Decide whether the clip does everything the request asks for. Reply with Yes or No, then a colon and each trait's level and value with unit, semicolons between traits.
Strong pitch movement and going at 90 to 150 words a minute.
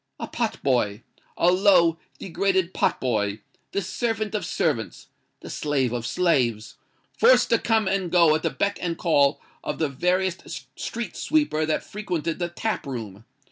Yes: wide, 6.2 semitones; average, 145 wpm